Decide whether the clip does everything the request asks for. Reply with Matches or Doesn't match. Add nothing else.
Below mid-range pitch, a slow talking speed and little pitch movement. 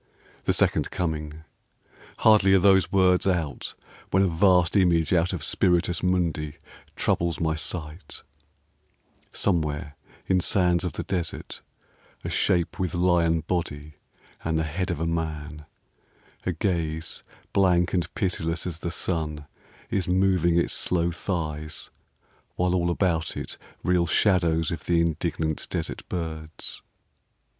Matches